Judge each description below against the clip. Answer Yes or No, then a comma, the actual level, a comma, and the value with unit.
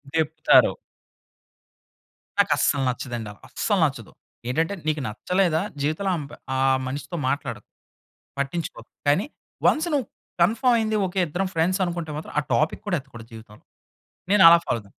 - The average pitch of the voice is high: No, medium, 160 Hz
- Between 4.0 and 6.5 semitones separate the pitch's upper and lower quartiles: Yes, average, 5.0 semitones